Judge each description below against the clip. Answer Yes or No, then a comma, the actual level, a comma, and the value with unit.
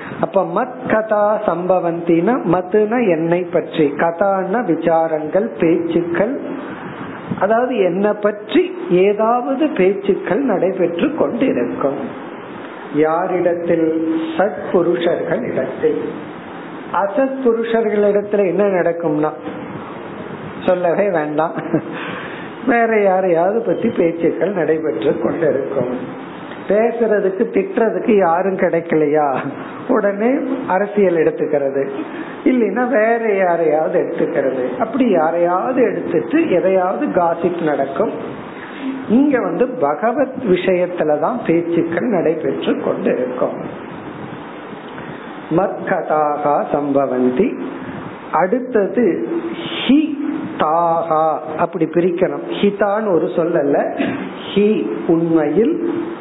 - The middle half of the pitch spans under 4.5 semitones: No, wide, 5.4 semitones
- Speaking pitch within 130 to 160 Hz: No, medium, 185 Hz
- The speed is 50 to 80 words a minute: Yes, slow, 75 wpm